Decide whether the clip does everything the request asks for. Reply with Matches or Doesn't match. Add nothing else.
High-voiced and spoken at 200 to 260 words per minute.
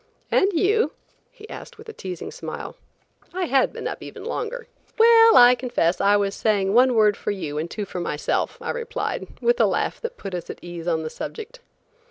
Matches